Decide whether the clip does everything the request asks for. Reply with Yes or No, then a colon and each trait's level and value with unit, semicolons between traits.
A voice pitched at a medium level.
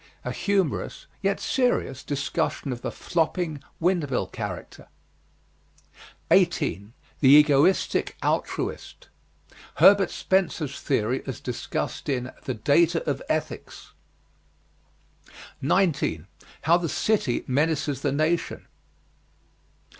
Yes: medium, 150 Hz